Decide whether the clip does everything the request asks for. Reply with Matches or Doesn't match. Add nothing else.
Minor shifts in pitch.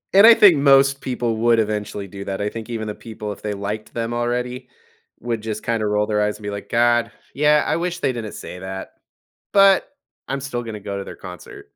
Doesn't match